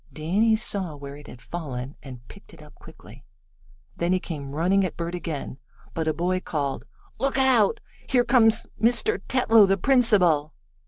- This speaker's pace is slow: No, average, 165 wpm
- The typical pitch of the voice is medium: Yes, medium, 180 Hz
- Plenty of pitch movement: Yes, wide, 7.0 semitones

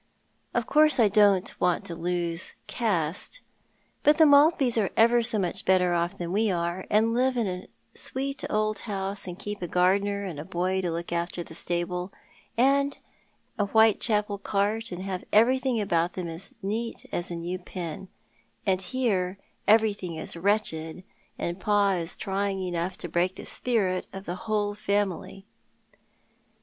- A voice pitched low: No, high, 195 Hz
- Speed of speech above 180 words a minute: No, average, 160 wpm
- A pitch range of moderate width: Yes, average, 3.5 semitones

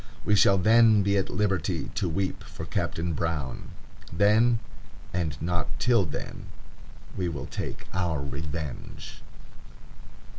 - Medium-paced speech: No, slow, 120 wpm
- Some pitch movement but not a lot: Yes, average, 4.2 semitones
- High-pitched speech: No, very low, 90 Hz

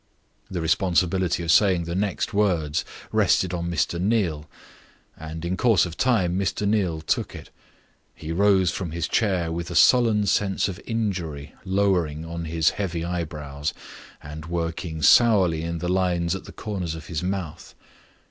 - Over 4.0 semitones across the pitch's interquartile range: No, average, 2.9 semitones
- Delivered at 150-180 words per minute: Yes, average, 155 wpm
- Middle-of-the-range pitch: No, very low, 85 Hz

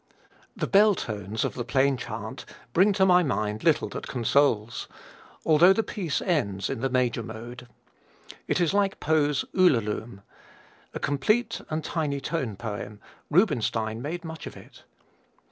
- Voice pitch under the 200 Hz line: Yes, medium, 140 Hz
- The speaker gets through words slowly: No, average, 145 wpm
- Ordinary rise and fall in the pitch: No, wide, 7.4 semitones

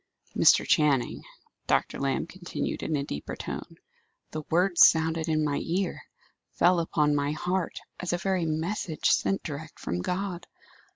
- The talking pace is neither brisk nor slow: Yes, average, 150 wpm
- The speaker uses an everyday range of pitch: Yes, average, 3.1 semitones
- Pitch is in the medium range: Yes, medium, 160 Hz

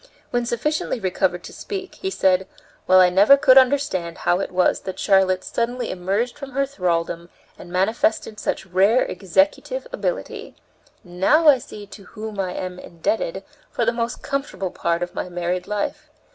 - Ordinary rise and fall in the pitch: No, wide, 6.2 semitones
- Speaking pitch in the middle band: No, high, 200 Hz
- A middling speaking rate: Yes, average, 165 wpm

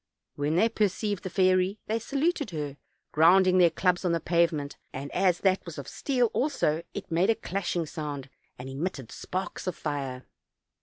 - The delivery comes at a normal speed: Yes, average, 170 wpm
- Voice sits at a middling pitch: Yes, medium, 175 Hz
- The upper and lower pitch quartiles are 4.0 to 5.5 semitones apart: Yes, average, 4.3 semitones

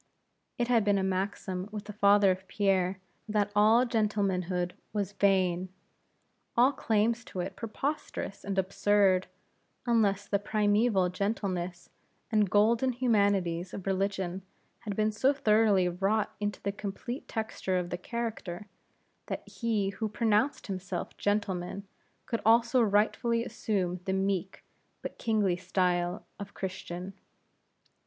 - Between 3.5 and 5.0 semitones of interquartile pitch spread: No, narrow, 2.6 semitones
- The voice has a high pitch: Yes, high, 200 Hz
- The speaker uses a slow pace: Yes, slow, 130 wpm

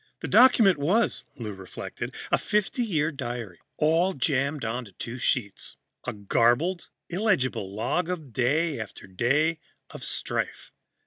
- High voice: No, medium, 140 Hz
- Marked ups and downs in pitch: Yes, wide, 6.8 semitones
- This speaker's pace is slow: Yes, slow, 130 wpm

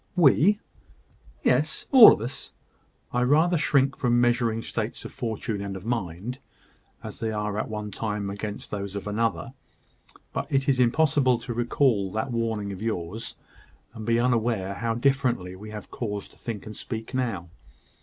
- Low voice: Yes, low, 115 Hz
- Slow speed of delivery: No, average, 165 wpm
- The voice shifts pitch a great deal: No, average, 3.3 semitones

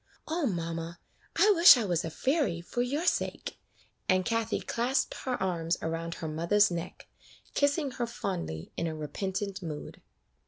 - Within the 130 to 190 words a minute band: Yes, average, 155 wpm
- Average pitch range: No, wide, 6.9 semitones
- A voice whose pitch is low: No, high, 190 Hz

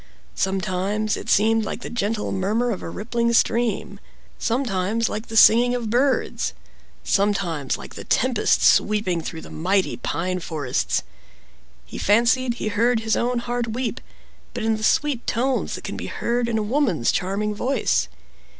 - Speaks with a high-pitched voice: Yes, high, 220 Hz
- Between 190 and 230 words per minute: No, average, 160 wpm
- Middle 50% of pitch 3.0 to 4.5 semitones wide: Yes, average, 3.6 semitones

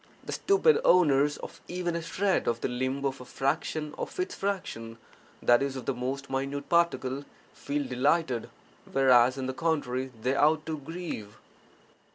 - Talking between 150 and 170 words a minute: Yes, average, 160 wpm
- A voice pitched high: No, medium, 140 Hz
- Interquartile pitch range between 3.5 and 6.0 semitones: Yes, average, 4.0 semitones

